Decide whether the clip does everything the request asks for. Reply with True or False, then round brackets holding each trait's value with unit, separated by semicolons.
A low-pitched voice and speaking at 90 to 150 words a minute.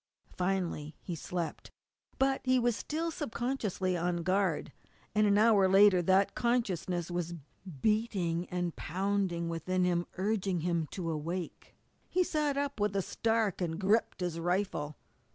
False (185 Hz; 140 wpm)